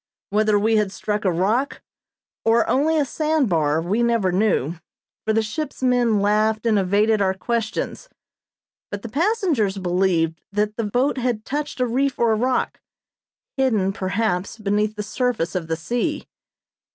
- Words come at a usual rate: Yes, average, 155 wpm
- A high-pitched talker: Yes, high, 215 Hz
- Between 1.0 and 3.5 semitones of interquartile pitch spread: No, average, 4.2 semitones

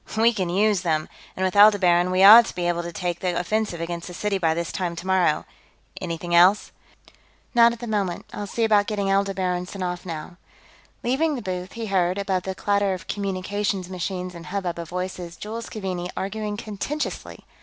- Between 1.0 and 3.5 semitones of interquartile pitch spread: Yes, average, 2.8 semitones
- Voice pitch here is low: No, high, 190 Hz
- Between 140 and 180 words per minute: No, average, 190 wpm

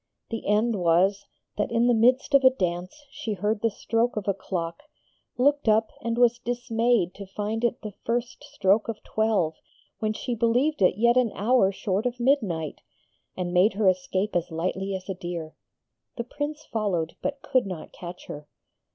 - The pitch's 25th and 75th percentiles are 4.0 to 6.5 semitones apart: Yes, average, 4.4 semitones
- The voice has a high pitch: Yes, high, 215 Hz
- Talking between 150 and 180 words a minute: Yes, average, 175 wpm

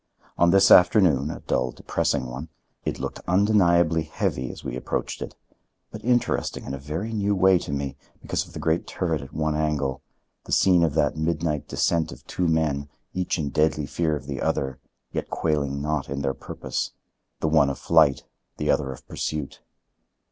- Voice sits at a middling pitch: No, very low, 75 Hz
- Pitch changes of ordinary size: Yes, average, 3.5 semitones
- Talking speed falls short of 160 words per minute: No, average, 175 wpm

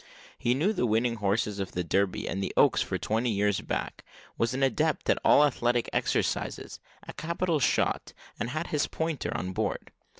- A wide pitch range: Yes, wide, 6.5 semitones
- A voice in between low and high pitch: No, low, 120 Hz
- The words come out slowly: No, average, 180 wpm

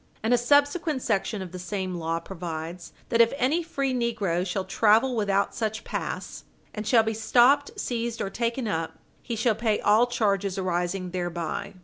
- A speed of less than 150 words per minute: No, average, 170 wpm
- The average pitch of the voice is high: Yes, high, 215 Hz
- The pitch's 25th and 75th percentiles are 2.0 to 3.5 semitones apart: No, average, 4.5 semitones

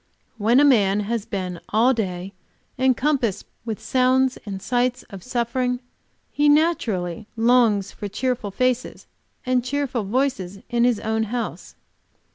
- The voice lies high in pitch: Yes, high, 235 Hz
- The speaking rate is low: Yes, slow, 130 wpm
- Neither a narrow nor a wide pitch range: Yes, average, 3.8 semitones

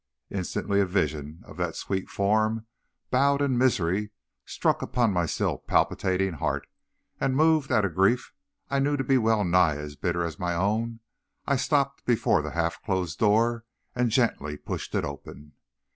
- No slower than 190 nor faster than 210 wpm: No, average, 165 wpm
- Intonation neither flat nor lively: No, wide, 6.1 semitones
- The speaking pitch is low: Yes, low, 105 Hz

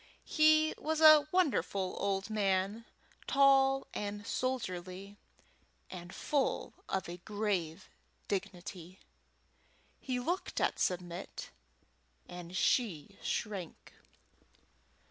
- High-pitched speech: Yes, high, 200 Hz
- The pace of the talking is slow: Yes, slow, 85 wpm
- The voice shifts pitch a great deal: Yes, wide, 6.6 semitones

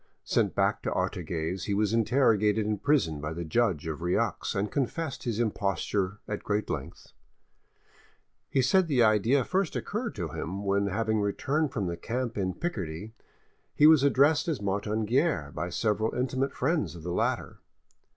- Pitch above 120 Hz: No, low, 105 Hz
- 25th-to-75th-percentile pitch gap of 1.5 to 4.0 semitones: No, wide, 5.5 semitones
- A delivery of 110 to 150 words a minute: No, average, 165 wpm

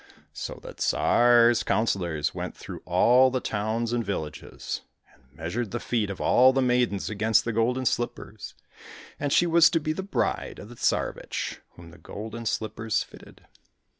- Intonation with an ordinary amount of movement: Yes, average, 3.3 semitones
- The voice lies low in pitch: Yes, low, 115 Hz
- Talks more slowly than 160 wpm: No, average, 165 wpm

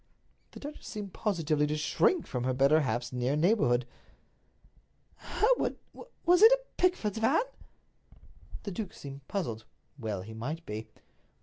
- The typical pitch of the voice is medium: Yes, medium, 155 Hz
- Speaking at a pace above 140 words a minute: No, slow, 135 wpm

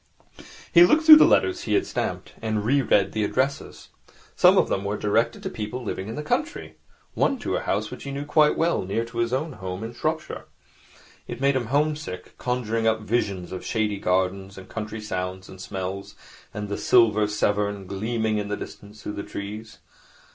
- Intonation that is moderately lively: Yes, average, 4.5 semitones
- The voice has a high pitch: No, low, 110 Hz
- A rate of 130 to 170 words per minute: No, average, 200 wpm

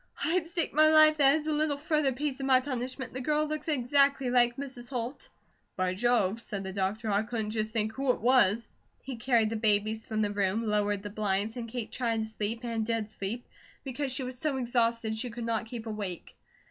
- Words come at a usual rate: No, fast, 215 wpm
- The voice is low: No, high, 235 Hz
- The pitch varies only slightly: No, average, 3.8 semitones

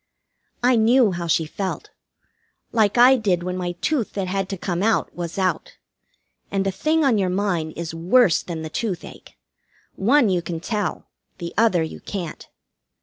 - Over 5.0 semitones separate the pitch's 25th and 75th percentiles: No, average, 4.4 semitones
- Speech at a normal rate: Yes, average, 170 wpm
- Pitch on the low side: No, high, 190 Hz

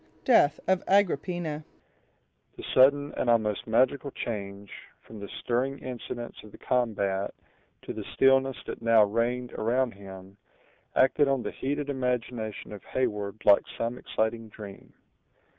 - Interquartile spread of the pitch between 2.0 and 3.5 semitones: No, average, 4.1 semitones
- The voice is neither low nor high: No, low, 120 Hz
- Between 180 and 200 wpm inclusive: No, slow, 135 wpm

